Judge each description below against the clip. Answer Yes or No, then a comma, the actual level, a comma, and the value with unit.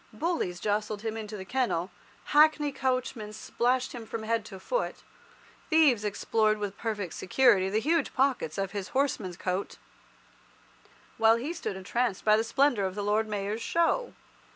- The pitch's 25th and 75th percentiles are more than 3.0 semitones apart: Yes, average, 4.5 semitones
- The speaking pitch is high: Yes, high, 220 Hz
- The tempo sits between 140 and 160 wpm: Yes, average, 155 wpm